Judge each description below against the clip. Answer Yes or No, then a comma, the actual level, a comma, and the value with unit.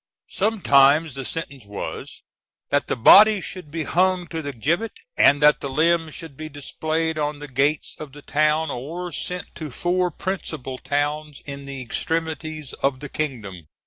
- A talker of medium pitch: Yes, medium, 150 Hz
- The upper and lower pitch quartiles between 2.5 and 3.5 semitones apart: Yes, average, 2.9 semitones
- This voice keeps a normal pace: Yes, average, 165 wpm